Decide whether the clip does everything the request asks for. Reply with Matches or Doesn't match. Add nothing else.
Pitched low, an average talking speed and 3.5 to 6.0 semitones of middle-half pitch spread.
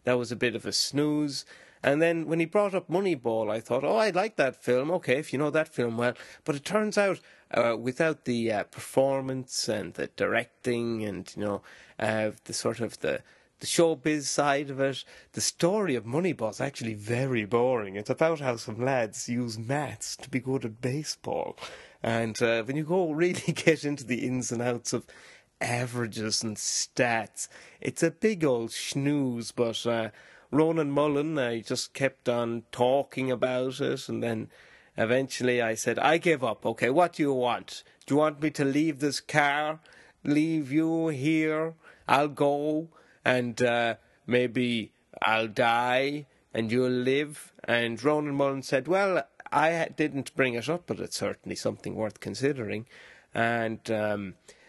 Matches